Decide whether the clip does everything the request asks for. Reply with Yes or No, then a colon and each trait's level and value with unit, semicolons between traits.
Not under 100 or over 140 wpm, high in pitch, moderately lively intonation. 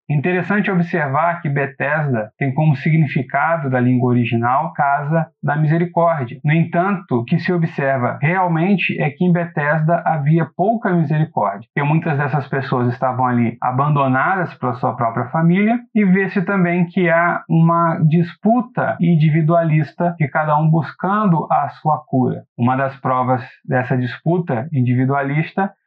No: average, 135 wpm; medium, 155 Hz; average, 4.4 semitones